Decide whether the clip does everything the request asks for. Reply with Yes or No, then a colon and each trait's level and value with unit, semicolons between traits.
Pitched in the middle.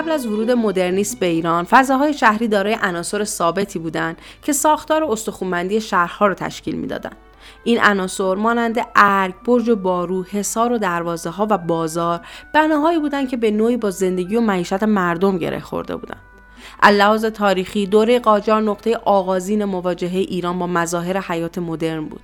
No: high, 200 Hz